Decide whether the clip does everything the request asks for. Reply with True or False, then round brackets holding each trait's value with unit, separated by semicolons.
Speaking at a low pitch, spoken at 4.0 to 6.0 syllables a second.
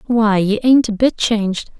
False (220 Hz; 4.6 syllables/s)